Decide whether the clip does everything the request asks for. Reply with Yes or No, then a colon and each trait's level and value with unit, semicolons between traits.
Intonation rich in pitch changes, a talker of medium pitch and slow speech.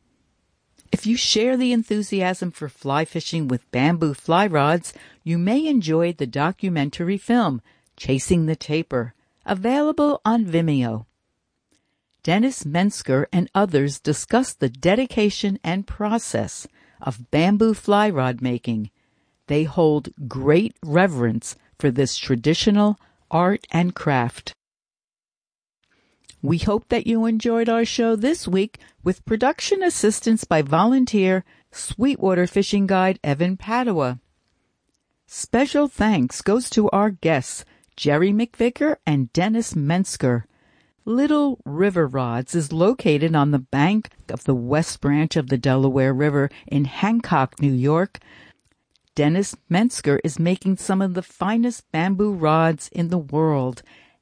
Yes: wide, 6.8 semitones; medium, 175 Hz; slow, 125 wpm